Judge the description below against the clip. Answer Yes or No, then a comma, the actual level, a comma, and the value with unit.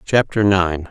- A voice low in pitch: Yes, very low, 95 Hz